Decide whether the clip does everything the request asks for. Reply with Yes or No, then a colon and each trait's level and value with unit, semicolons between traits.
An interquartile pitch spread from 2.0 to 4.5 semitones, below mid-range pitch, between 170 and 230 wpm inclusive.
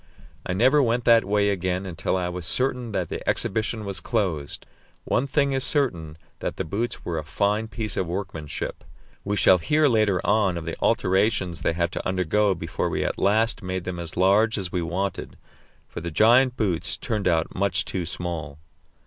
Yes: average, 4.2 semitones; very low, 95 Hz; average, 190 wpm